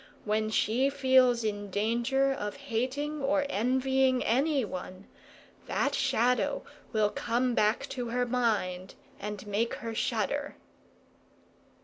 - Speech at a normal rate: No, slow, 110 wpm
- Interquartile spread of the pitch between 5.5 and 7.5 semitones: No, average, 3.8 semitones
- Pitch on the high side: Yes, high, 240 Hz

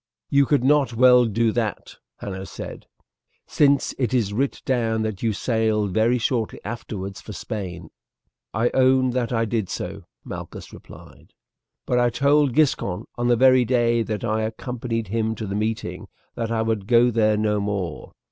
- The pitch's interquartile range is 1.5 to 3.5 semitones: Yes, narrow, 2.6 semitones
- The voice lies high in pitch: No, low, 115 Hz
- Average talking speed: Yes, average, 165 wpm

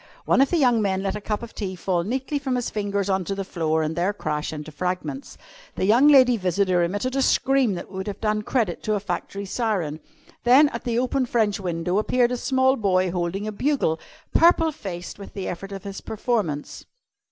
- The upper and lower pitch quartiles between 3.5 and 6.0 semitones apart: Yes, average, 5.1 semitones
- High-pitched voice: Yes, high, 205 Hz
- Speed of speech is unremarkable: No, fast, 210 wpm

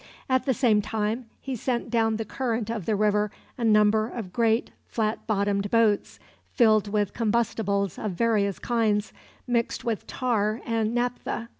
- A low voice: No, high, 220 Hz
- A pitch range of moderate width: No, narrow, 2.0 semitones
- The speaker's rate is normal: Yes, average, 155 wpm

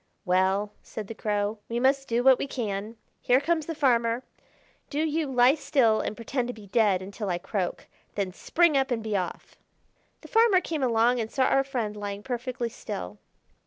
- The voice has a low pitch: No, high, 235 Hz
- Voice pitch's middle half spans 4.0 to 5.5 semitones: Yes, average, 4.6 semitones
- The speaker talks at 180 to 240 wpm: Yes, average, 190 wpm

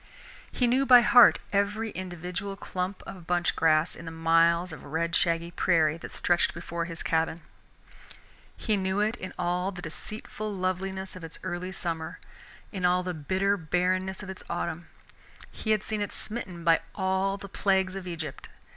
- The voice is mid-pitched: Yes, medium, 180 Hz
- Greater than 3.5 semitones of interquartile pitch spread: No, narrow, 2.6 semitones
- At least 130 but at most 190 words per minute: Yes, average, 170 wpm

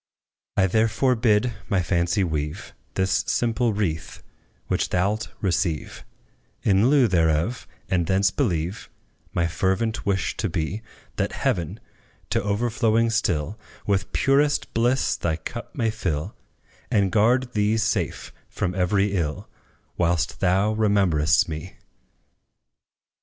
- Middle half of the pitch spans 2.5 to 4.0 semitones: No, average, 4.5 semitones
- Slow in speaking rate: Yes, slow, 120 wpm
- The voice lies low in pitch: Yes, low, 100 Hz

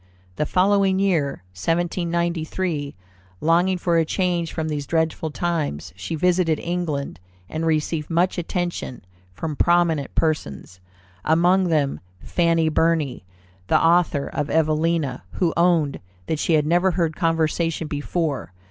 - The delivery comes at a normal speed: No, slow, 125 wpm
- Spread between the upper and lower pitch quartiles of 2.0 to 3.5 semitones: Yes, narrow, 2.4 semitones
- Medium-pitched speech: Yes, medium, 165 Hz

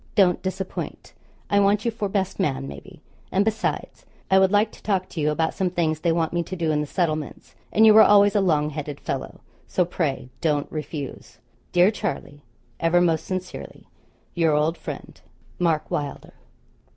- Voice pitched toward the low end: No, medium, 175 Hz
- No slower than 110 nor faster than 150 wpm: No, average, 180 wpm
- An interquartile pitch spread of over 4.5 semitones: No, average, 4.1 semitones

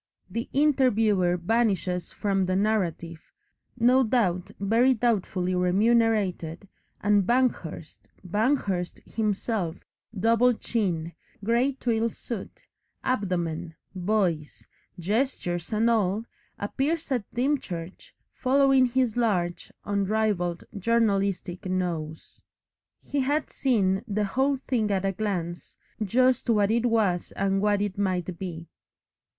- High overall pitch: Yes, high, 205 Hz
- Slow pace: Yes, slow, 105 wpm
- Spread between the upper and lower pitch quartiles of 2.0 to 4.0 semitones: No, average, 4.5 semitones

